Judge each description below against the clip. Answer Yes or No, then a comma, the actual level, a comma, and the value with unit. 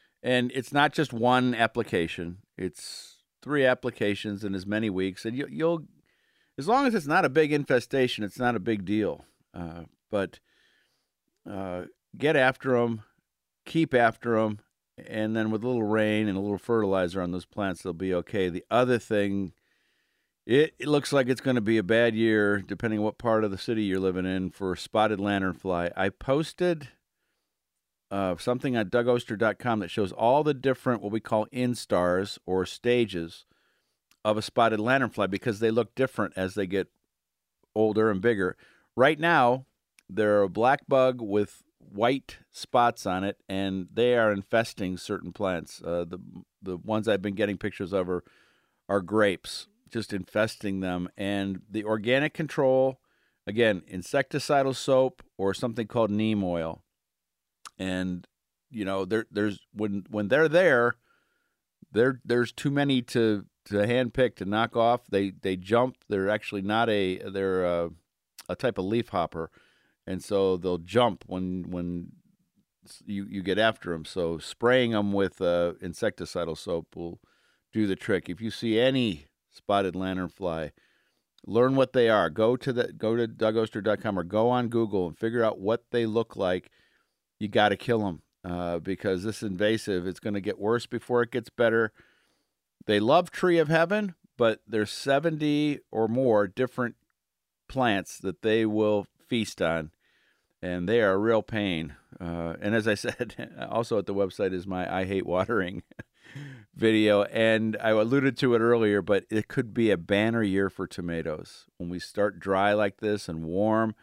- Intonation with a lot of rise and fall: No, average, 4.1 semitones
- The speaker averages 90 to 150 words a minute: No, average, 165 wpm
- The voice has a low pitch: Yes, low, 105 Hz